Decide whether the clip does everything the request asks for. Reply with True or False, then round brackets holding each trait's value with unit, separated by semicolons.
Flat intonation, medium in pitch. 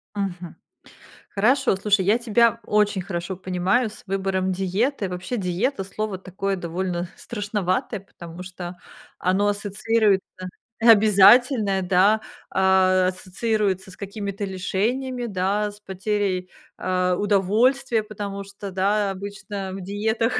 False (2.3 semitones; 195 Hz)